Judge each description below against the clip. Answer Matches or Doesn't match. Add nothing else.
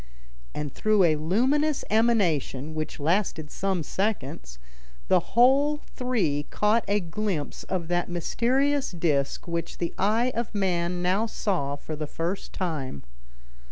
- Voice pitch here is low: Doesn't match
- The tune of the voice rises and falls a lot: Matches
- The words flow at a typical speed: Doesn't match